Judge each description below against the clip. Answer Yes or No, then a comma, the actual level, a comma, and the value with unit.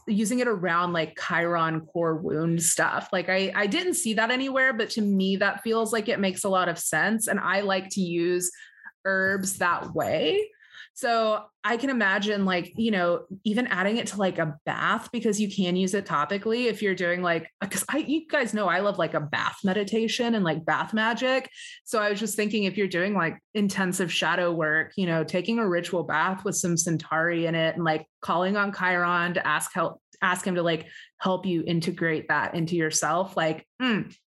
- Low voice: No, high, 190 Hz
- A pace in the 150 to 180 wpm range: No, fast, 205 wpm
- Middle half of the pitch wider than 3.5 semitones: Yes, average, 4.3 semitones